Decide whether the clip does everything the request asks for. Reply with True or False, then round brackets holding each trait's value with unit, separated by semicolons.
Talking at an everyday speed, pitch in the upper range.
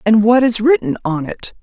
False (220 wpm; 220 Hz)